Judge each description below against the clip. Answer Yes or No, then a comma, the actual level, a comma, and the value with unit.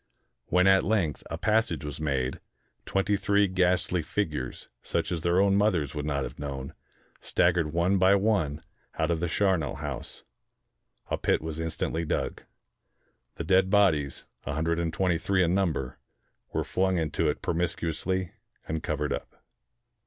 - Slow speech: No, average, 160 wpm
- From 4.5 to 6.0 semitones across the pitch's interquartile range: No, average, 3.7 semitones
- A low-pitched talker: Yes, very low, 85 Hz